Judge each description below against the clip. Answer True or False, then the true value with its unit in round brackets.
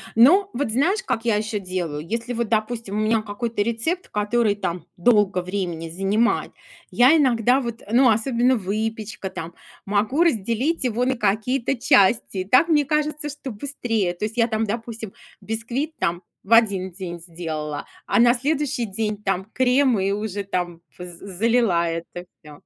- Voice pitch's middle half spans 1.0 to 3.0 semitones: False (4.3 semitones)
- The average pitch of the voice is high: True (220 Hz)